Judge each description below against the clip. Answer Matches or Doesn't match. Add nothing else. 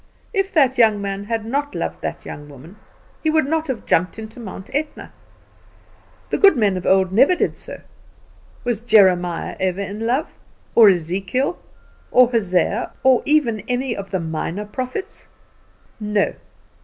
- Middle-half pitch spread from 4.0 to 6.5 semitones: Matches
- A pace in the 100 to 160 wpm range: Matches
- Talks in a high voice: Matches